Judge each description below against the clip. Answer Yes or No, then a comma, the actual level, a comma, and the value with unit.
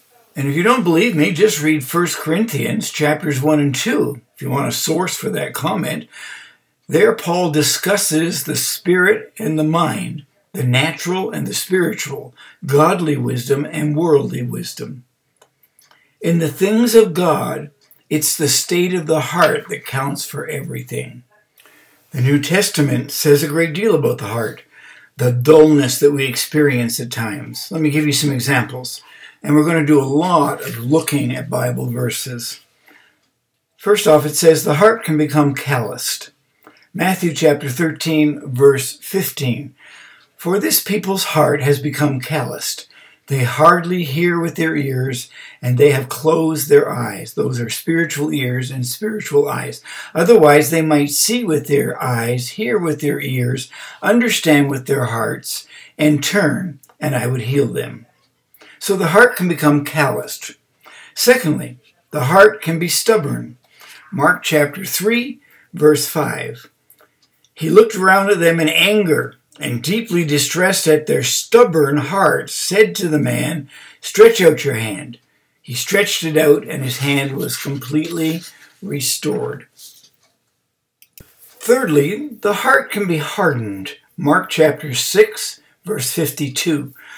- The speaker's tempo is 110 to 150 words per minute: Yes, average, 145 wpm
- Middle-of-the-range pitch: Yes, medium, 155 Hz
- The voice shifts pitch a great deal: No, average, 4.1 semitones